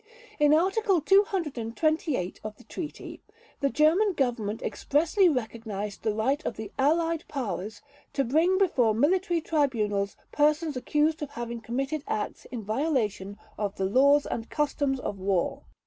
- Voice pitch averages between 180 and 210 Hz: No, very high, 275 Hz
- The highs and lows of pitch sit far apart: Yes, wide, 6.3 semitones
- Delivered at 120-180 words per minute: Yes, average, 140 wpm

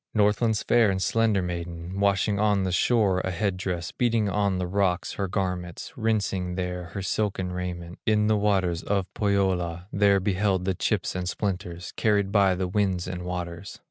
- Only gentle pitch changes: Yes, narrow, 2.3 semitones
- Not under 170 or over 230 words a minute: Yes, average, 175 wpm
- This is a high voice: No, very low, 95 Hz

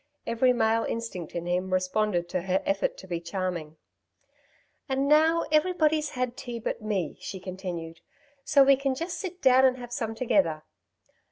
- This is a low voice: No, high, 225 Hz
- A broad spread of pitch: Yes, wide, 6.7 semitones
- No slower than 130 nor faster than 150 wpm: No, average, 165 wpm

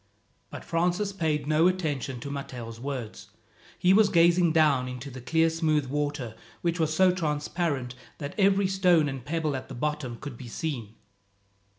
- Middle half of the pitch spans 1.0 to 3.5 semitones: No, average, 4.3 semitones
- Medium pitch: Yes, medium, 150 Hz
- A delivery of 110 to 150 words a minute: No, average, 165 wpm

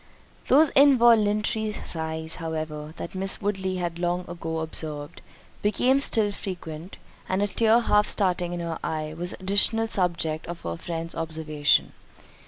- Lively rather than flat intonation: No, average, 4.5 semitones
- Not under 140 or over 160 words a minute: Yes, average, 150 wpm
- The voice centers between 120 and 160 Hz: No, medium, 175 Hz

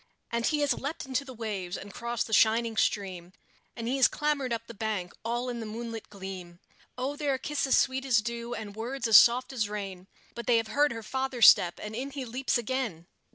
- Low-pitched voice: No, high, 235 Hz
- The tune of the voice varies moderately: Yes, average, 3.6 semitones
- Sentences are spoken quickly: Yes, fast, 220 wpm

